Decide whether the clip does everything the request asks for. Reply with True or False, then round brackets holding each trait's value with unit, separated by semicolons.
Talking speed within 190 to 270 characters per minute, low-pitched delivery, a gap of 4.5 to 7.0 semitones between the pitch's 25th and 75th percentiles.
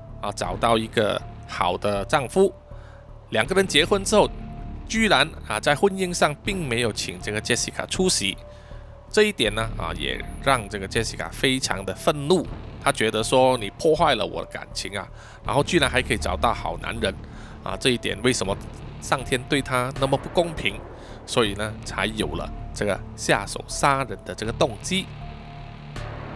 True (250 characters per minute; 115 Hz; 5.1 semitones)